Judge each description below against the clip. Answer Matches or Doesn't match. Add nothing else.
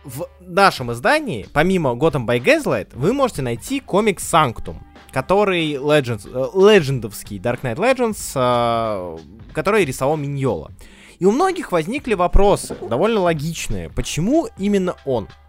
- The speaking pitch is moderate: Matches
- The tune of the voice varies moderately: Doesn't match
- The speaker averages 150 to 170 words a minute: Doesn't match